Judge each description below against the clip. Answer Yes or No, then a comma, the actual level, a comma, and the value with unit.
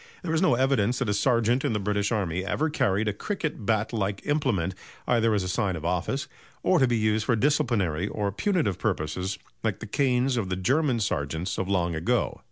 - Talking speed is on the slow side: No, fast, 205 wpm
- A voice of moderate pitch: No, low, 105 Hz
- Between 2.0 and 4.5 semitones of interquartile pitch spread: No, average, 5.1 semitones